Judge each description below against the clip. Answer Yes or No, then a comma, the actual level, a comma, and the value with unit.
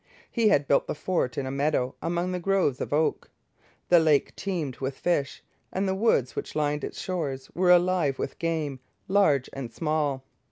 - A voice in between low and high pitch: Yes, medium, 155 Hz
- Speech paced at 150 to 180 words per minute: Yes, average, 175 wpm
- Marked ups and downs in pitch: No, average, 4.6 semitones